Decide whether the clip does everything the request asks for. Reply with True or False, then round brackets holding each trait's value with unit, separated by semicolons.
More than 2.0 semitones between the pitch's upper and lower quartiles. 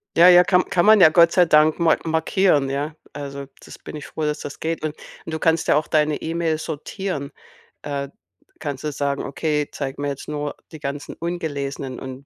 True (2.7 semitones)